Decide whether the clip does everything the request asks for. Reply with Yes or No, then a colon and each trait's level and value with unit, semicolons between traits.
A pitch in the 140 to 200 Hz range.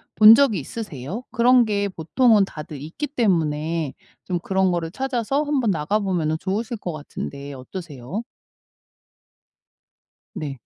Yes: high, 190 Hz